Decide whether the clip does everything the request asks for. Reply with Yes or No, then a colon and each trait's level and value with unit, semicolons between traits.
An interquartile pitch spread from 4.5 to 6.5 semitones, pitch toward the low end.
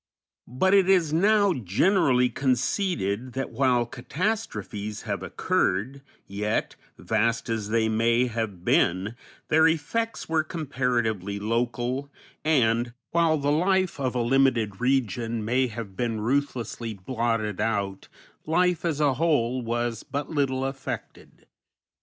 Yes: average, 4.8 semitones; low, 125 Hz